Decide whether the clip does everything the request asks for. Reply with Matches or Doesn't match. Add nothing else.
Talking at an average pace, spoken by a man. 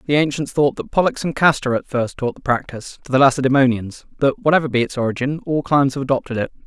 Doesn't match